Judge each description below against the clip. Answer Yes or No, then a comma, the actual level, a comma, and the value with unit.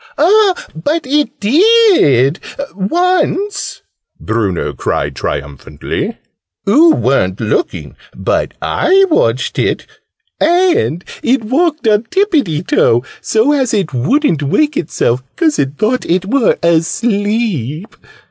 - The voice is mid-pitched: No, high, 220 Hz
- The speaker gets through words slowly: Yes, slow, 110 wpm